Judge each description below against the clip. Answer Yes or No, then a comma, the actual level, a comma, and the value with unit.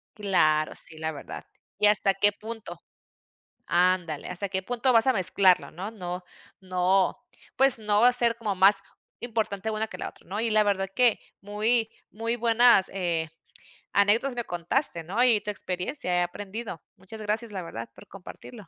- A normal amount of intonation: Yes, average, 3.8 semitones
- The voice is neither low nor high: No, high, 205 Hz